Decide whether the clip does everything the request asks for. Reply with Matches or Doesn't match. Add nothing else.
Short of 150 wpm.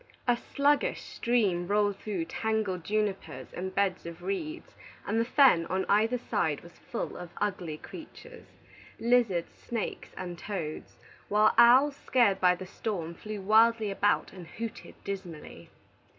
Matches